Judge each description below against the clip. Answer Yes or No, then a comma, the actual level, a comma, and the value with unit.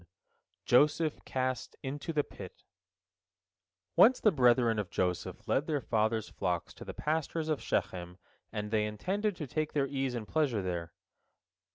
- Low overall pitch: Yes, low, 130 Hz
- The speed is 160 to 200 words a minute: No, average, 150 wpm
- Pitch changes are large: Yes, wide, 6.3 semitones